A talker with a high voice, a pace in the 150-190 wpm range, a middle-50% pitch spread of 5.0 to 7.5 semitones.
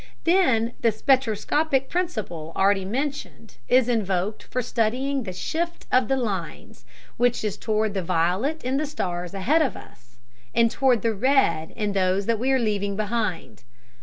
Yes: high, 225 Hz; average, 160 wpm; average, 5.3 semitones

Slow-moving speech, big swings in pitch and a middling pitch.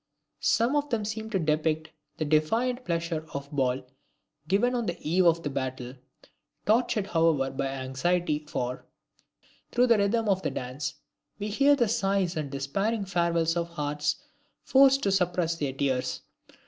No: average, 155 wpm; wide, 6.4 semitones; medium, 170 Hz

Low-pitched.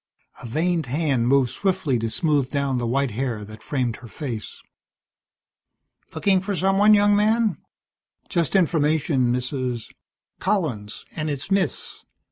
No: medium, 145 Hz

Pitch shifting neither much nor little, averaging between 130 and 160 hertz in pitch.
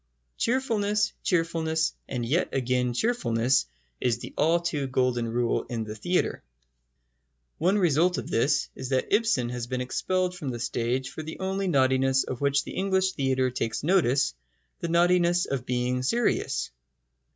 No: wide, 6.1 semitones; medium, 140 Hz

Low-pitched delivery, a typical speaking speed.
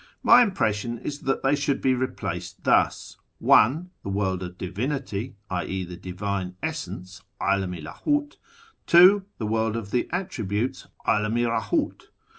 Yes: low, 110 Hz; average, 150 wpm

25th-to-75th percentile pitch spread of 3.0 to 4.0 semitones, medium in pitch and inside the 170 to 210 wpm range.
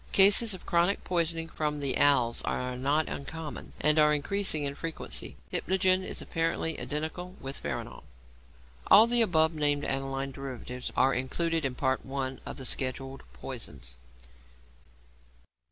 No: average, 3.7 semitones; medium, 150 Hz; slow, 135 wpm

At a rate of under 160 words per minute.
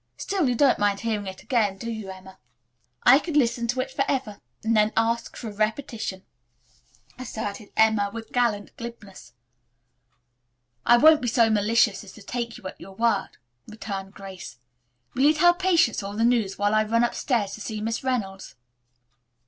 No: average, 175 wpm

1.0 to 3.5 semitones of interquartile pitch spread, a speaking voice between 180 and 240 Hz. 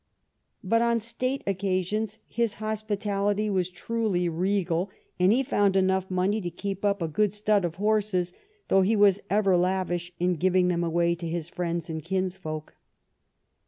Yes: average, 2.9 semitones; high, 190 Hz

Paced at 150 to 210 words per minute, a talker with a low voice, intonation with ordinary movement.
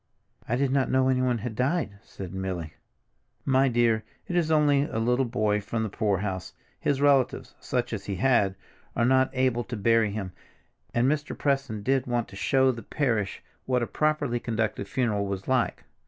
Yes: average, 170 wpm; low, 120 Hz; average, 4.0 semitones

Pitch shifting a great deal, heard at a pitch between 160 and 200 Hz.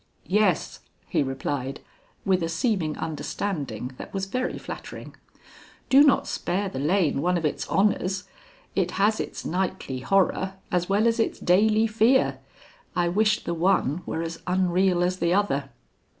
No: average, 3.7 semitones; medium, 185 Hz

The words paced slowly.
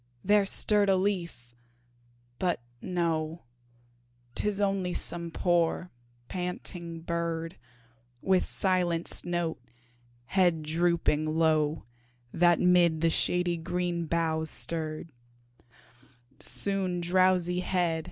Yes: slow, 85 wpm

